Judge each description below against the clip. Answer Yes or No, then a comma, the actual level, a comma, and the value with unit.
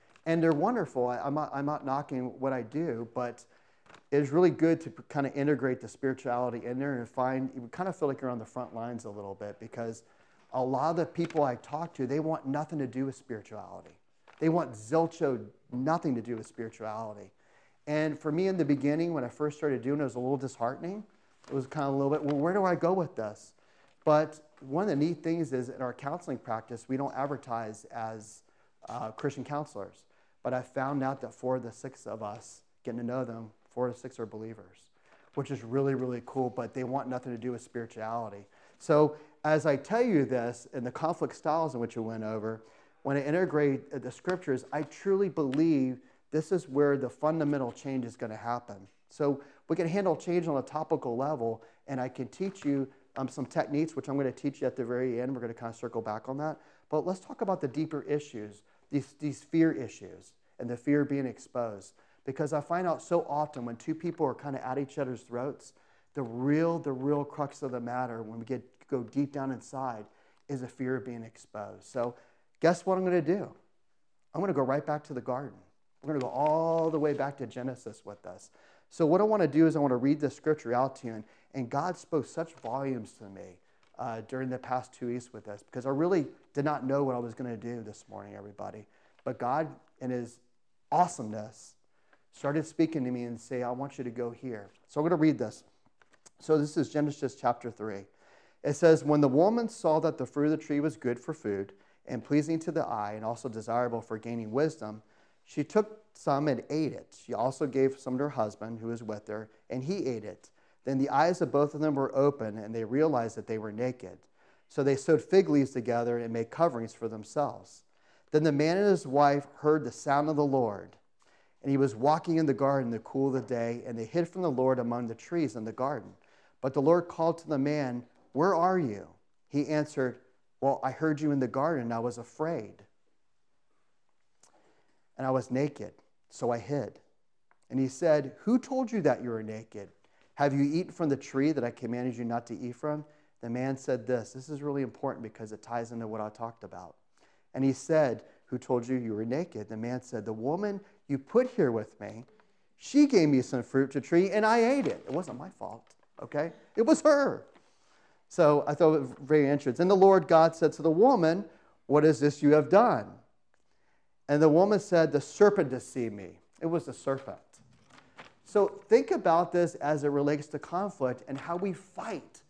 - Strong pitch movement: No, average, 4.2 semitones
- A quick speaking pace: Yes, fast, 220 wpm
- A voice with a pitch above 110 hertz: Yes, low, 135 Hz